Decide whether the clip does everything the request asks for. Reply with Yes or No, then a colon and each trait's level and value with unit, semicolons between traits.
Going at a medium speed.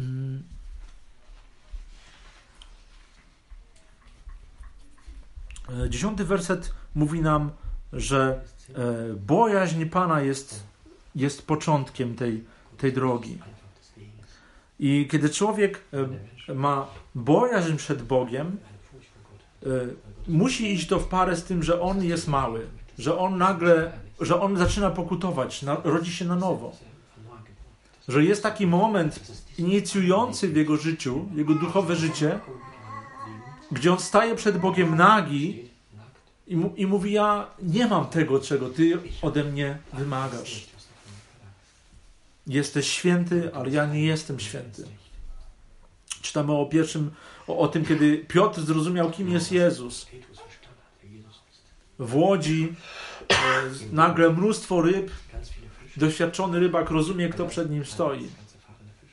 No: slow, 100 wpm